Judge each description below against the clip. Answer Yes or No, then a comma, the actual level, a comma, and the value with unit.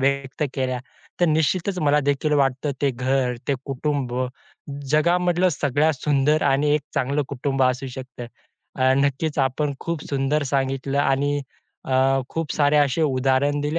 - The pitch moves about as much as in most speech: No, narrow, 2.1 semitones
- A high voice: No, medium, 140 Hz